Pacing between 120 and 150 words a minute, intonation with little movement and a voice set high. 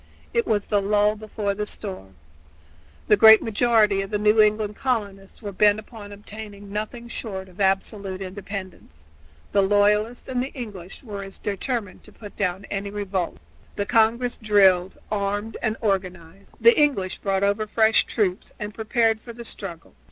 No: average, 165 wpm; narrow, 2.0 semitones; high, 205 Hz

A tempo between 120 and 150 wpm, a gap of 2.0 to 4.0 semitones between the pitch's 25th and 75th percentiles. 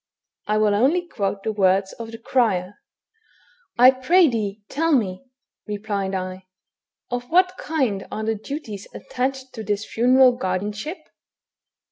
No: average, 145 wpm; average, 4.6 semitones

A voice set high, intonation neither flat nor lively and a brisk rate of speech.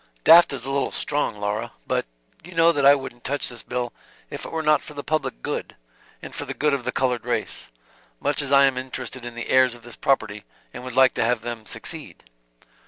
No: low, 130 Hz; average, 3.2 semitones; fast, 230 wpm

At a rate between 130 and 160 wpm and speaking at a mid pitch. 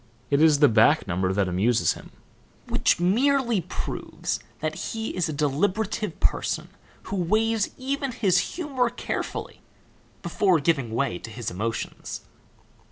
Yes: slow, 135 wpm; medium, 175 Hz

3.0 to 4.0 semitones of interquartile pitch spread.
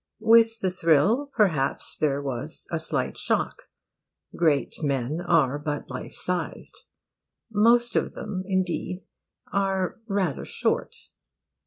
No: wide, 5.5 semitones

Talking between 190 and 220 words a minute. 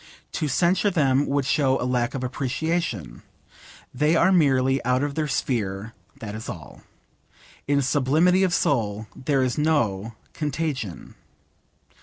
No: slow, 135 wpm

